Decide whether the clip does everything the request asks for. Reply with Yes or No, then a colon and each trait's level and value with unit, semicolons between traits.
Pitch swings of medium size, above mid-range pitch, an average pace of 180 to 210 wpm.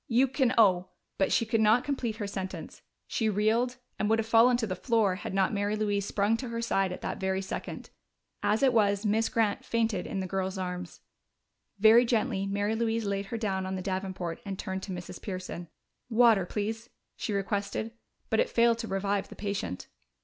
Yes: average, 3.0 semitones; high, 205 Hz; average, 200 wpm